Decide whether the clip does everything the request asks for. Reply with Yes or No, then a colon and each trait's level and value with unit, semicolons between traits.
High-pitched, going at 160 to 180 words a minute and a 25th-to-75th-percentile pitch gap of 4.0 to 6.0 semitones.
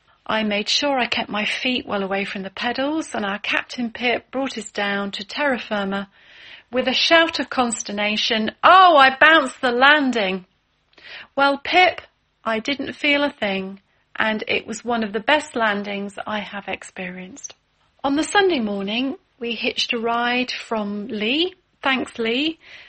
Yes: high, 235 Hz; average, 165 wpm; average, 5.0 semitones